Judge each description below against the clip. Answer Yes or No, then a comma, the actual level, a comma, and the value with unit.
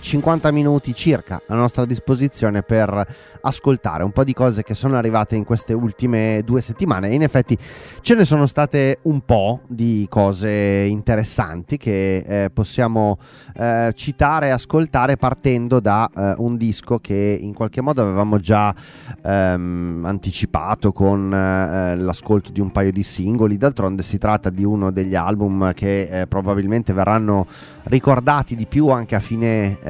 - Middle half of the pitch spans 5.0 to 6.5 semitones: No, average, 4.4 semitones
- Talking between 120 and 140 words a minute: No, average, 155 wpm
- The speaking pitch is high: No, low, 110 Hz